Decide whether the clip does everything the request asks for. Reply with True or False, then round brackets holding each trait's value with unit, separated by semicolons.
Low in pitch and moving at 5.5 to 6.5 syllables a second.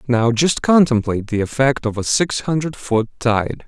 False (125 Hz; 4.7 syllables/s)